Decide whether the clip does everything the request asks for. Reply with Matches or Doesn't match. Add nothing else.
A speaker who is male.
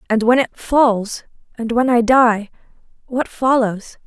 Doesn't match